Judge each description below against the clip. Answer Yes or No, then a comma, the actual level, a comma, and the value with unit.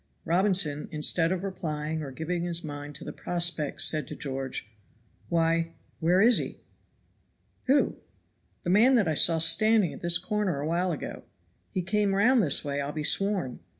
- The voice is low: No, medium, 170 Hz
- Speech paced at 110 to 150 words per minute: No, average, 170 wpm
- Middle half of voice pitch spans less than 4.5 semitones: Yes, average, 4.1 semitones